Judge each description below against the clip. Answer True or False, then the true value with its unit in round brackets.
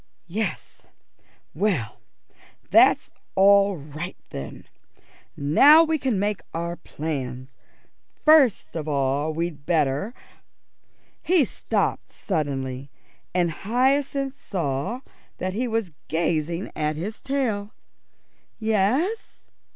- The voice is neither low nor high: True (180 Hz)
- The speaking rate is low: True (95 wpm)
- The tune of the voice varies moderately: False (7.0 semitones)